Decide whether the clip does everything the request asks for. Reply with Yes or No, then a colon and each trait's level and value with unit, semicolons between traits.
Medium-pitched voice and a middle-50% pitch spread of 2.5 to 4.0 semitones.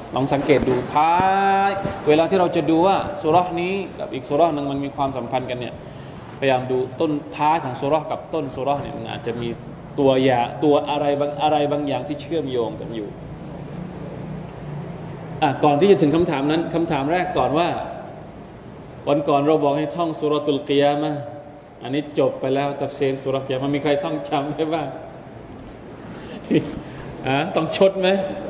Yes: medium, 150 Hz; average, 2.8 semitones